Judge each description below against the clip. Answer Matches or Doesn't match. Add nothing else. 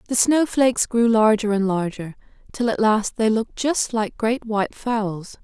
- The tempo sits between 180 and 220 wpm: Matches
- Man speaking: Doesn't match